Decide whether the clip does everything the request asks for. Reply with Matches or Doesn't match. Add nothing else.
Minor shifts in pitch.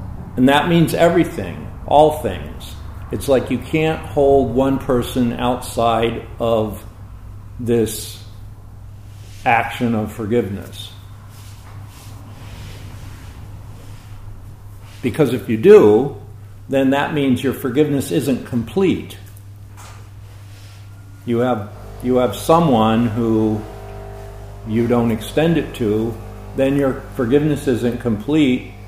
Doesn't match